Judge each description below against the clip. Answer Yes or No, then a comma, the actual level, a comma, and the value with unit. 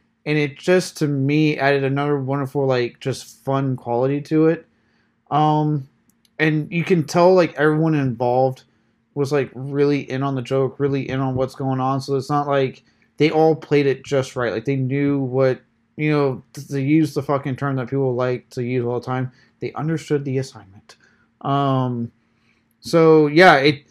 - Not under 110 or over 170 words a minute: No, average, 180 wpm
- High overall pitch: No, medium, 140 Hz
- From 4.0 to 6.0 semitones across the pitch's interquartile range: No, narrow, 2.4 semitones